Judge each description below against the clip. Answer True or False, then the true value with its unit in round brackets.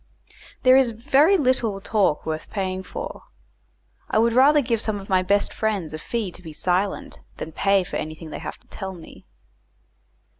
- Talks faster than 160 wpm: True (180 wpm)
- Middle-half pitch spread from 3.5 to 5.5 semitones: True (4.4 semitones)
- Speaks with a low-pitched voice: False (200 Hz)